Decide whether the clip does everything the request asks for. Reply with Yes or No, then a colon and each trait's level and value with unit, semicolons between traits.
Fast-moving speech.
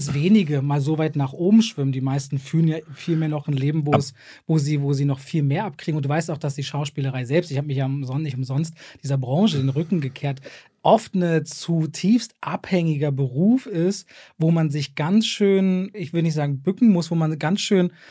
Yes: fast, 220 wpm